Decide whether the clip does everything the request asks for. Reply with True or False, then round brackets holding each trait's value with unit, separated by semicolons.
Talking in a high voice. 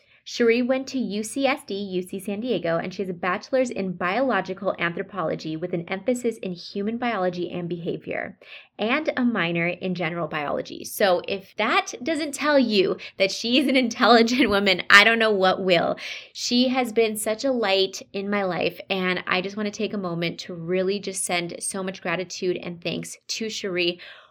True (195 Hz)